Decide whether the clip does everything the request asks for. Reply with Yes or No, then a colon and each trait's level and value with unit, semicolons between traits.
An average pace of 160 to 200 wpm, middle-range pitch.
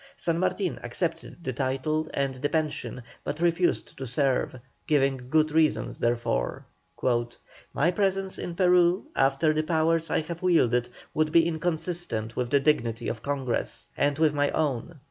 No: average, 150 wpm; medium, 155 Hz